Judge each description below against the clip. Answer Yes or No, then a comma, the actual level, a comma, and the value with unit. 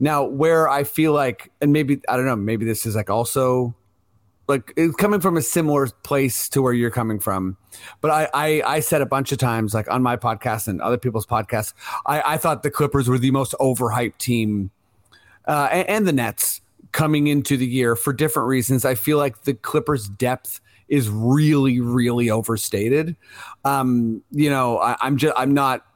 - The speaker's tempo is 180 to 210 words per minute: Yes, average, 195 wpm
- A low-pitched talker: Yes, low, 130 Hz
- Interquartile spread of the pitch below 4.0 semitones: No, average, 4.3 semitones